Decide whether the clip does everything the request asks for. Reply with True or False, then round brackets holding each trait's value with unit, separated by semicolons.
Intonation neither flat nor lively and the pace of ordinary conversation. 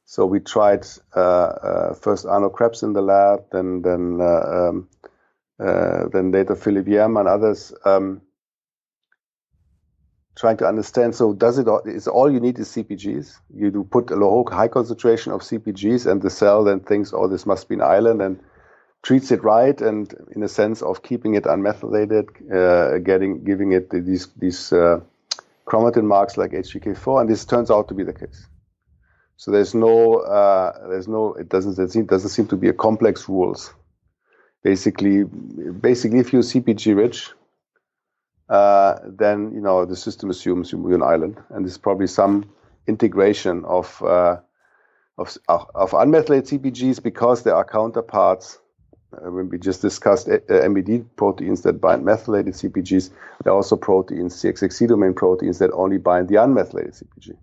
True (3.5 semitones; 165 wpm)